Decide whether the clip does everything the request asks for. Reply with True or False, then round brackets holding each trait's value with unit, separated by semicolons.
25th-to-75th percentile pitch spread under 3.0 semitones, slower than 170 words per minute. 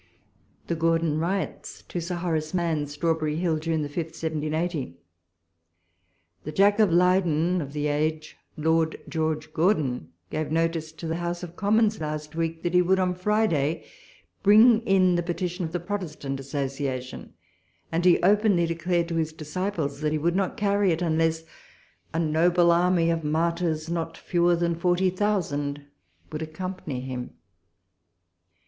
True (2.5 semitones; 155 wpm)